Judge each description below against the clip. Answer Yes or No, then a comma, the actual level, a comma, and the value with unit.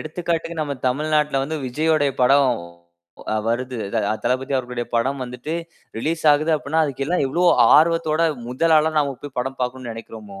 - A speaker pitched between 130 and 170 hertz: Yes, medium, 140 Hz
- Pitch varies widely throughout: No, average, 3.8 semitones